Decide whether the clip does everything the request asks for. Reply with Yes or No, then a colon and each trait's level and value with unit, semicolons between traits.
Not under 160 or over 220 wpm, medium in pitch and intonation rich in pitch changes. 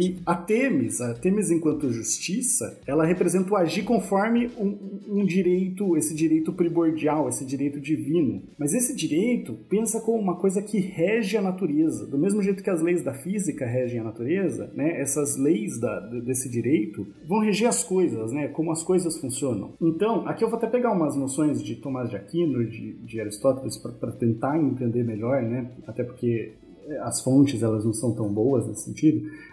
Yes: average, 180 wpm; medium, 160 Hz; wide, 7.1 semitones